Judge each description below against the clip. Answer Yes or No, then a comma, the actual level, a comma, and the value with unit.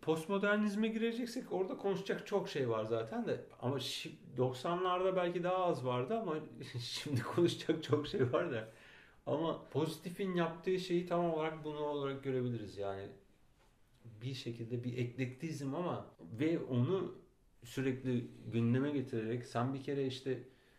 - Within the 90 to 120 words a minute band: No, average, 135 wpm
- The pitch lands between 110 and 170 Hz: Yes, medium, 140 Hz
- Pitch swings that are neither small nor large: No, wide, 6.3 semitones